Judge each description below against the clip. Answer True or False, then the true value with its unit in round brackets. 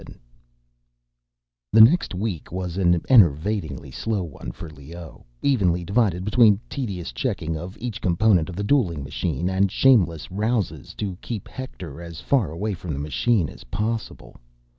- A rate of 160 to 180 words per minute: False (150 wpm)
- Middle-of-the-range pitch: False (90 Hz)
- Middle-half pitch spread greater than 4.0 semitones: True (5.0 semitones)